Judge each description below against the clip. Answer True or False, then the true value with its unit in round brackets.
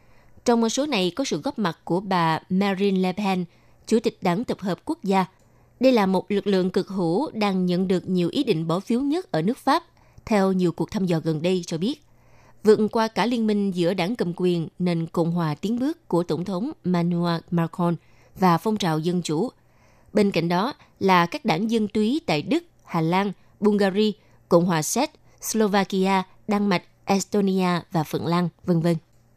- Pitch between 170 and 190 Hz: True (185 Hz)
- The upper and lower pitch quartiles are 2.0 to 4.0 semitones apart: True (3.6 semitones)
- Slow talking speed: False (200 wpm)